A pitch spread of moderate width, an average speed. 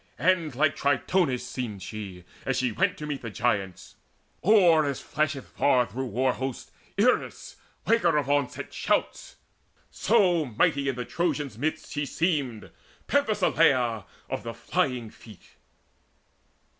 No: average, 5.0 semitones; slow, 130 wpm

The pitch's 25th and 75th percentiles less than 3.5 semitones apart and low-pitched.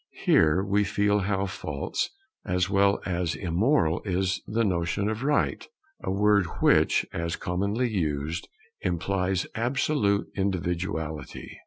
Yes: average, 3.0 semitones; very low, 95 Hz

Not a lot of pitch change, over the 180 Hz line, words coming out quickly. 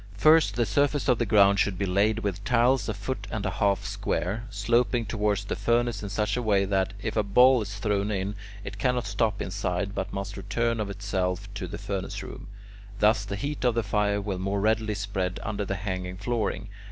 No: narrow, 2.3 semitones; low, 100 Hz; fast, 210 wpm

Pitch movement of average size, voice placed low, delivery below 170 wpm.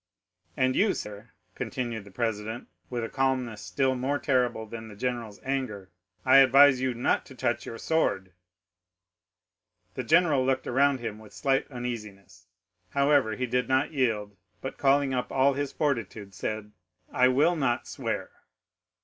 Yes: average, 3.6 semitones; low, 125 Hz; average, 150 wpm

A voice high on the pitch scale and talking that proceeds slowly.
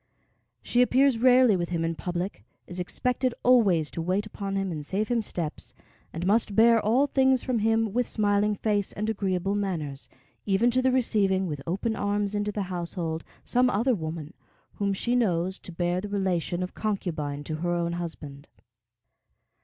No: high, 195 Hz; average, 175 wpm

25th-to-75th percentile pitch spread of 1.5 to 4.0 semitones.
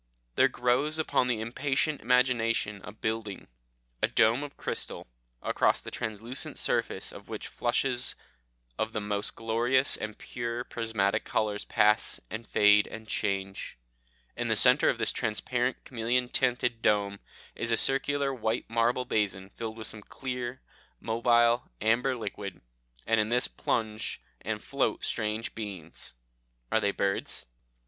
Yes: narrow, 2.6 semitones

